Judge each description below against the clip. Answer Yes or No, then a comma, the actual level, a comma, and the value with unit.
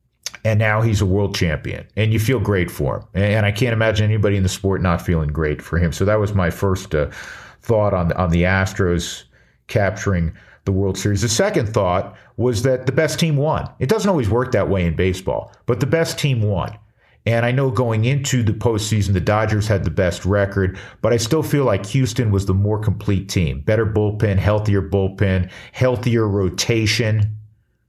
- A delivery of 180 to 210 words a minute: Yes, average, 200 wpm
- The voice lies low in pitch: Yes, low, 105 Hz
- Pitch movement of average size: Yes, average, 3.3 semitones